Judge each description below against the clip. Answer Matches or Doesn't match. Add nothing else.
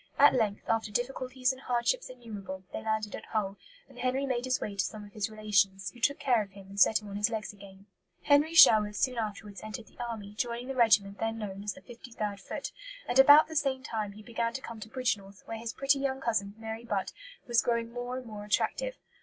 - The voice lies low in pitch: Doesn't match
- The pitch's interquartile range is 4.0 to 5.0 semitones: Doesn't match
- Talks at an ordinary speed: Doesn't match